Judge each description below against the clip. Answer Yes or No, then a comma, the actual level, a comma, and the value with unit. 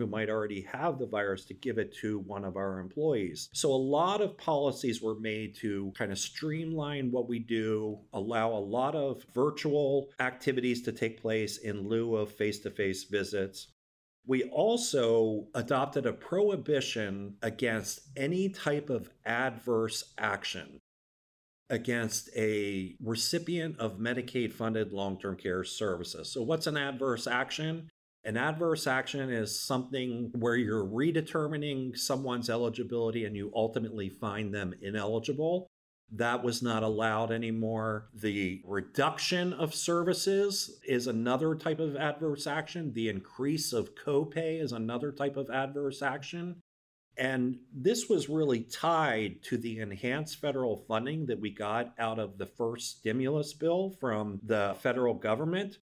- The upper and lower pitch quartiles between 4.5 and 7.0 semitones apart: Yes, average, 5.1 semitones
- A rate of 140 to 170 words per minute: Yes, average, 145 wpm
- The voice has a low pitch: Yes, low, 125 Hz